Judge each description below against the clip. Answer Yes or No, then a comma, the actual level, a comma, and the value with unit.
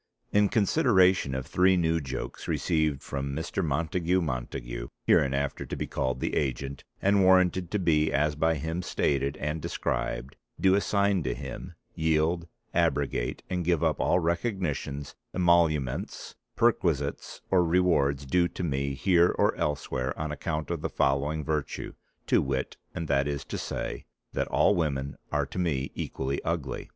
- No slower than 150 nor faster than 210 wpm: Yes, average, 155 wpm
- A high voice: No, very low, 80 Hz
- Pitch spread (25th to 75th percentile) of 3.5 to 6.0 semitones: Yes, average, 4.4 semitones